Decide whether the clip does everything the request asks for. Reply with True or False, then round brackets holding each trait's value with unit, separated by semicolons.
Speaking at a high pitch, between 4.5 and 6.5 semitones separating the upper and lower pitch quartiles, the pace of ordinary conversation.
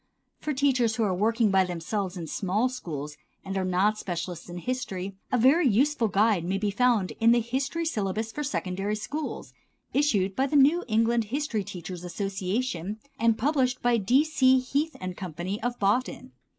True (220 Hz; 5.1 semitones; 175 wpm)